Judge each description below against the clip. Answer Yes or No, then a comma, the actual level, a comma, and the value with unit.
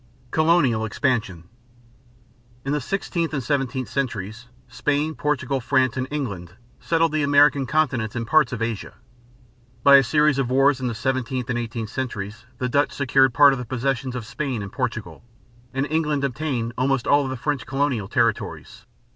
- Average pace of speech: Yes, average, 165 wpm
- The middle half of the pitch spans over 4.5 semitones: No, average, 3.3 semitones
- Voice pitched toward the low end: Yes, low, 130 Hz